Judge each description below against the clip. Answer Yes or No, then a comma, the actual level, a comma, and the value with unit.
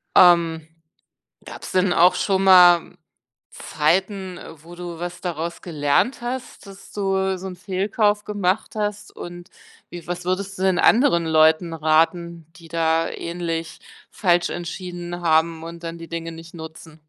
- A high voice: No, medium, 175 Hz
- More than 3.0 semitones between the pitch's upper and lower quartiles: No, narrow, 2.4 semitones